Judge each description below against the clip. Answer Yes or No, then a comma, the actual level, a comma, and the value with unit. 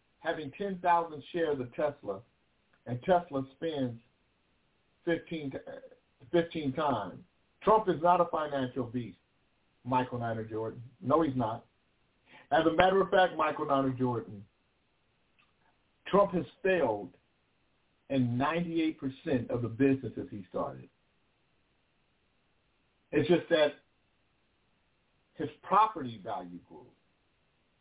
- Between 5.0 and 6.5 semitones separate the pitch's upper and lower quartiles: Yes, wide, 5.4 semitones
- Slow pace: Yes, slow, 105 wpm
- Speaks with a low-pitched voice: No, medium, 145 Hz